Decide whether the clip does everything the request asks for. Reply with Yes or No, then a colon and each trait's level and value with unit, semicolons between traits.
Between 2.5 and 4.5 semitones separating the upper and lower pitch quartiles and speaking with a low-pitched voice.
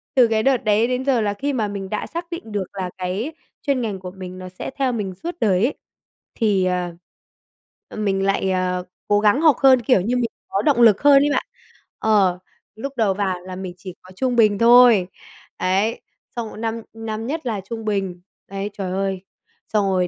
No: average, 4.2 semitones; high, 210 Hz